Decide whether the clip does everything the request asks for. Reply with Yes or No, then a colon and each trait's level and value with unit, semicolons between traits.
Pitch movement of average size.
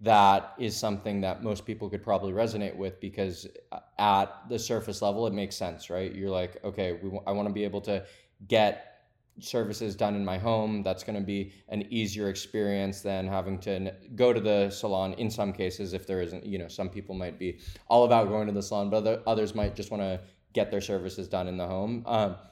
No: narrow, 2.0 semitones